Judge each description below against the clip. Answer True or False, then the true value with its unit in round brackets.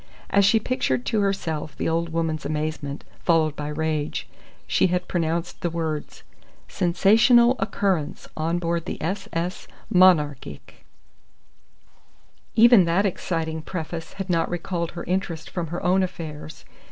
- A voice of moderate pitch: True (170 Hz)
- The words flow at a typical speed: False (130 wpm)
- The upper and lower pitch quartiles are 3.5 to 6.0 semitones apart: False (2.9 semitones)